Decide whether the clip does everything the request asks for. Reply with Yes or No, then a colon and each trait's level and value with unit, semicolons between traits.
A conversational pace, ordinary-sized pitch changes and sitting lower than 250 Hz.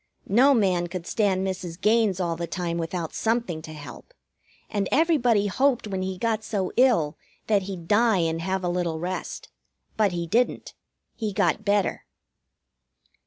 Yes: average, 160 wpm; average, 4.1 semitones; high, 190 Hz